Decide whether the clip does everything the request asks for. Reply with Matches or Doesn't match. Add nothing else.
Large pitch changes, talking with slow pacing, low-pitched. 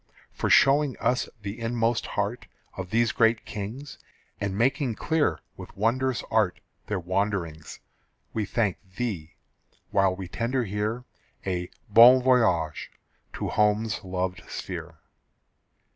Doesn't match